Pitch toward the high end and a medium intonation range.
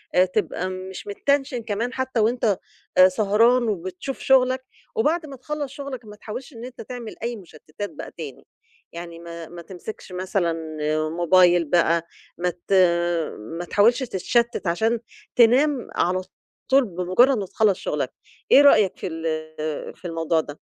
No: high, 205 Hz; wide, 5.9 semitones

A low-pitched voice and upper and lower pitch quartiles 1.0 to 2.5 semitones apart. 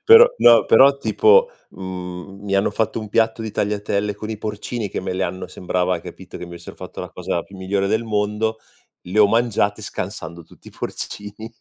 No: low, 105 Hz; average, 2.9 semitones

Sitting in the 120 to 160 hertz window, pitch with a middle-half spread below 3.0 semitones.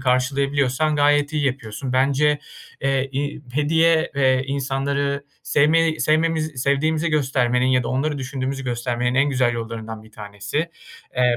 Yes: low, 135 Hz; narrow, 2.6 semitones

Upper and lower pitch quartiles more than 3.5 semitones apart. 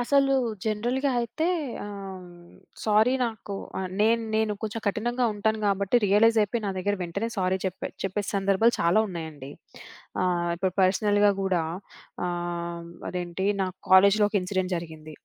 No: average, 3.2 semitones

